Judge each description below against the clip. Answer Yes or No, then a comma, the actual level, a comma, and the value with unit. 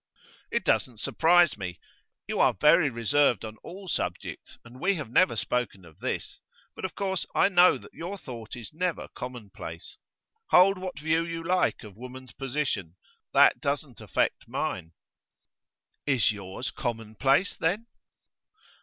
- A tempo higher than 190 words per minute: No, average, 145 wpm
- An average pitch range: No, wide, 7.7 semitones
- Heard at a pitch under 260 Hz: Yes, low, 135 Hz